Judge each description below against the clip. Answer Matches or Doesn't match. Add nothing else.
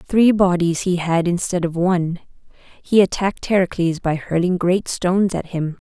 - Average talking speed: Matches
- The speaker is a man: Doesn't match